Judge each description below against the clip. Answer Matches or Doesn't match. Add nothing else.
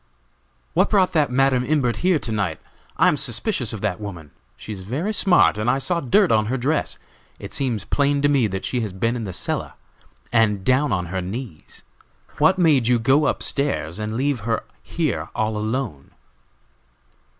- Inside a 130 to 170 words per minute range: Doesn't match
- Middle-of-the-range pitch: Doesn't match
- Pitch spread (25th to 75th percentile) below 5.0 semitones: Doesn't match